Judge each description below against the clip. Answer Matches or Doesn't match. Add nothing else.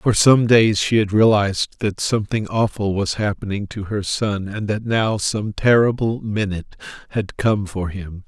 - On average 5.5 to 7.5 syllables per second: Doesn't match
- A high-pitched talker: Doesn't match